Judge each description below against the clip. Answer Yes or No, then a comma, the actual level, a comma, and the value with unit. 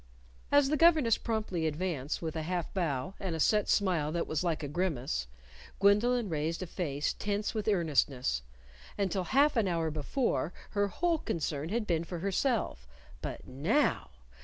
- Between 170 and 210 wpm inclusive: No, average, 160 wpm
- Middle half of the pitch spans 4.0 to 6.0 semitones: Yes, wide, 5.4 semitones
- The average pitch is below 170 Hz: No, medium, 180 Hz